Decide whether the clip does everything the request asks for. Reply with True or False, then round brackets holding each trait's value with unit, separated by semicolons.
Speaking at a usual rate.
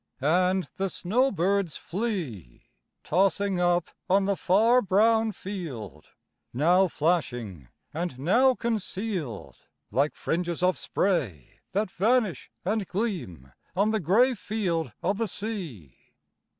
False (110 wpm)